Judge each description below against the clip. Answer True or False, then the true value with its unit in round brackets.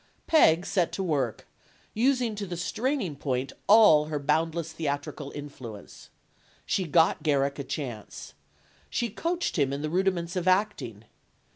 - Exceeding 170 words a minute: False (140 wpm)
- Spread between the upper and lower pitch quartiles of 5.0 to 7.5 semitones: True (5.5 semitones)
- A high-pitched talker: False (160 Hz)